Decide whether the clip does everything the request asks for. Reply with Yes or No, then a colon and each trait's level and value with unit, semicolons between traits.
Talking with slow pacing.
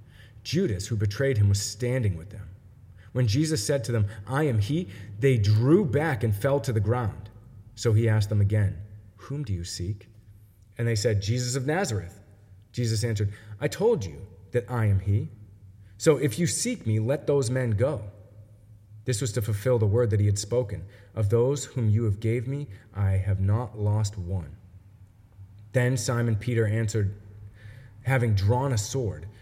No: average, 175 wpm